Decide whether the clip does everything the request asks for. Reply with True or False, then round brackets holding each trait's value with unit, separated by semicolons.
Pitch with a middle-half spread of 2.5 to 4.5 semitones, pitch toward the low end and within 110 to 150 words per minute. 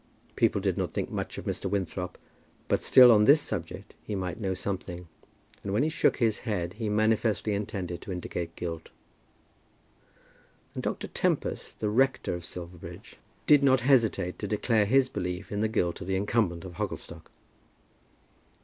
False (3.8 semitones; 100 Hz; 165 wpm)